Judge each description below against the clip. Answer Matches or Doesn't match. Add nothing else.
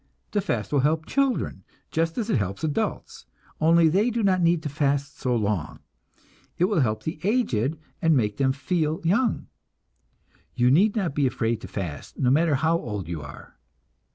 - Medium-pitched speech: Matches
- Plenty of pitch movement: Matches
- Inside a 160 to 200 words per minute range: Matches